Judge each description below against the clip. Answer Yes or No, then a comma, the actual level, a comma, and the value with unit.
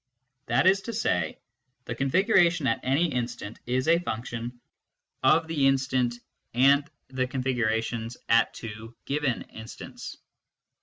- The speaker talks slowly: Yes, slow, 120 wpm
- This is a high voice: No, low, 130 Hz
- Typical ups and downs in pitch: Yes, average, 4.1 semitones